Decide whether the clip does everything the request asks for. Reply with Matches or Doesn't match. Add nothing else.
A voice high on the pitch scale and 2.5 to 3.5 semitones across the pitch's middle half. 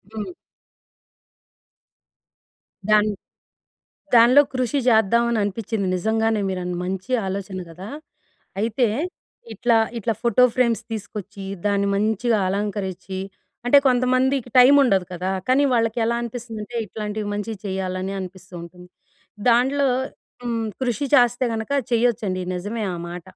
Doesn't match